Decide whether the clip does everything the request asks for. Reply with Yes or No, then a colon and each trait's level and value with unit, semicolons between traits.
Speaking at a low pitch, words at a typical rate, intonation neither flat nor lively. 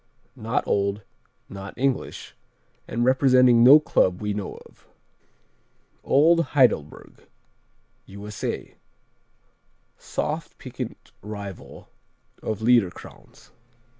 No: low, 110 Hz; slow, 85 wpm; average, 4.1 semitones